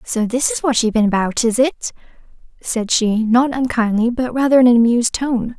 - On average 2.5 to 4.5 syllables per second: No, 5.4 syllables/s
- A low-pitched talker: No, high, 240 Hz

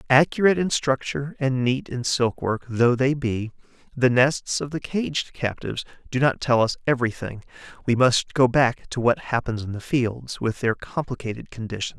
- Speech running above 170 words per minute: Yes, average, 180 wpm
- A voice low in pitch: Yes, low, 125 Hz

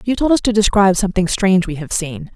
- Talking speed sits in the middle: No, fast, 255 wpm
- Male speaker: No, female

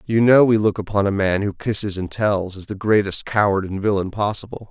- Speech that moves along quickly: Yes, fast, 230 wpm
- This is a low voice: Yes, low, 100 Hz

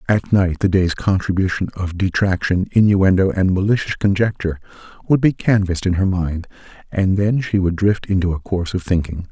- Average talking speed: Yes, average, 175 wpm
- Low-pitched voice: Yes, very low, 95 Hz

